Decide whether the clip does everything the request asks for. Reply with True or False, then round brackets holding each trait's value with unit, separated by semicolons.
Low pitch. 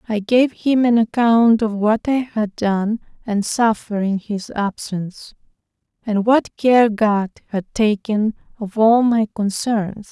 False (220 Hz)